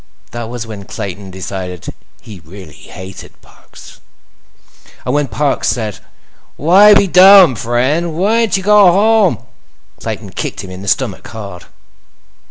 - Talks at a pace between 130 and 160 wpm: Yes, slow, 135 wpm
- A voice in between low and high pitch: No, low, 120 Hz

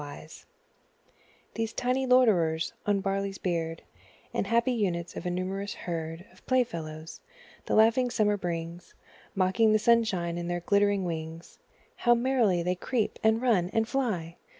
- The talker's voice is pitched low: No, high, 195 Hz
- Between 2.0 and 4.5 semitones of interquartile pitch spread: No, average, 4.9 semitones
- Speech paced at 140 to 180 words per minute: Yes, average, 150 wpm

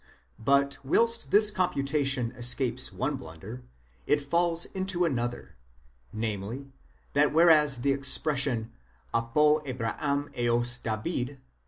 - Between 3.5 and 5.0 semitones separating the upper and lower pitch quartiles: Yes, average, 3.8 semitones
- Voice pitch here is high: No, low, 135 Hz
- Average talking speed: No, slow, 110 wpm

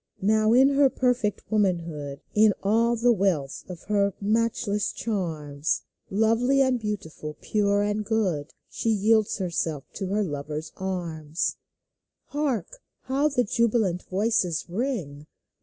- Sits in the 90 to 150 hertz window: No, high, 205 Hz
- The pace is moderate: No, slow, 130 wpm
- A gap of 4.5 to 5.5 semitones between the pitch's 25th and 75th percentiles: Yes, average, 5.1 semitones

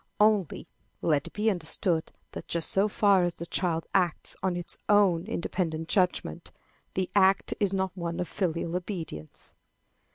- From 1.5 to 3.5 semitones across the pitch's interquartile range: Yes, average, 2.7 semitones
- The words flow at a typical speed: Yes, average, 155 wpm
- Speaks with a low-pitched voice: No, medium, 180 Hz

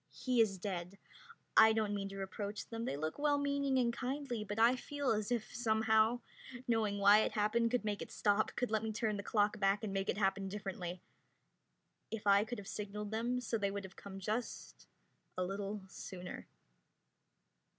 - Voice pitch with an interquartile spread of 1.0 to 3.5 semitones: Yes, average, 2.7 semitones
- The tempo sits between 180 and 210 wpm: Yes, average, 190 wpm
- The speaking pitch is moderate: No, high, 210 Hz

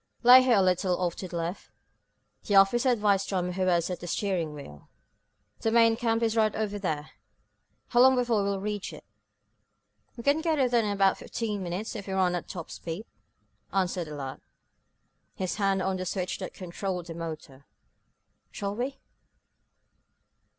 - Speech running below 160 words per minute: No, average, 175 wpm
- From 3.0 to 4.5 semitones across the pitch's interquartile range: Yes, average, 4.1 semitones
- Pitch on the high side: Yes, high, 195 Hz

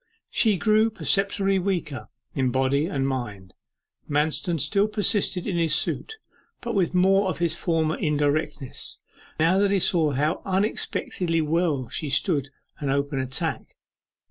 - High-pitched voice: No, medium, 165 Hz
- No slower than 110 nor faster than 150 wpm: Yes, average, 140 wpm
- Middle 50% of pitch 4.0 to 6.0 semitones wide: Yes, average, 5.3 semitones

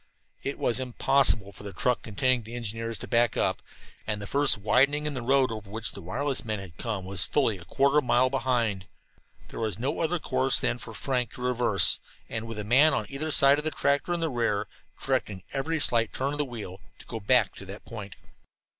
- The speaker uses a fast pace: Yes, fast, 225 wpm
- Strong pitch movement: No, average, 4.4 semitones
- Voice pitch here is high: No, low, 120 Hz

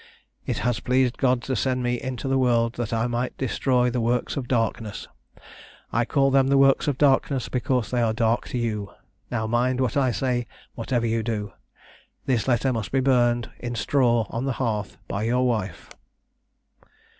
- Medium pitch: No, low, 120 Hz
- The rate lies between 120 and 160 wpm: No, average, 180 wpm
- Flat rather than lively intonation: Yes, narrow, 2.2 semitones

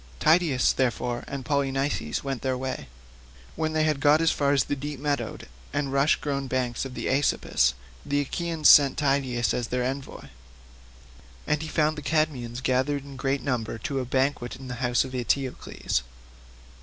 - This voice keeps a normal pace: Yes, average, 170 wpm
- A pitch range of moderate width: No, narrow, 2.3 semitones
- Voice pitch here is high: No, low, 135 Hz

